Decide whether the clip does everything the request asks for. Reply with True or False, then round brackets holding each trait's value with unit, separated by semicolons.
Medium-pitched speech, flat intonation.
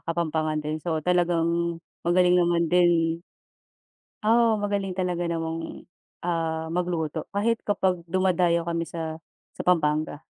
True (170 Hz; 1.7 semitones)